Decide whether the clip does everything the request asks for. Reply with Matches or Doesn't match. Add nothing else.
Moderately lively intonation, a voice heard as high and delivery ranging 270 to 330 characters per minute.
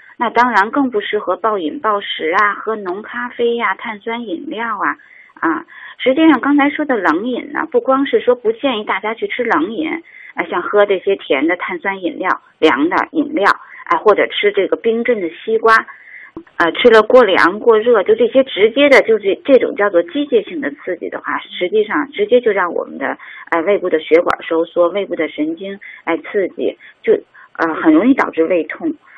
Doesn't match